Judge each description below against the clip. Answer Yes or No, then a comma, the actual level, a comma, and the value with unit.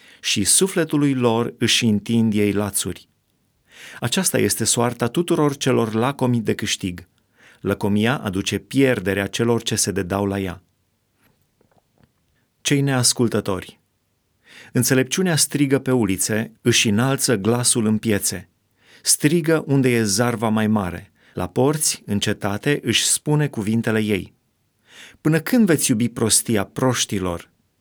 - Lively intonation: No, average, 4.2 semitones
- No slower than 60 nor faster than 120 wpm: Yes, slow, 115 wpm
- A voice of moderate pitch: No, low, 115 Hz